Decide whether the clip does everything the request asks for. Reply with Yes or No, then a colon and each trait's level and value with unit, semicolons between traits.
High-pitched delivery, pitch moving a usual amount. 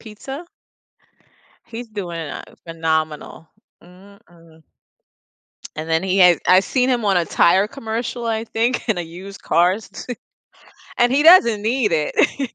No: high, 200 Hz; wide, 5.7 semitones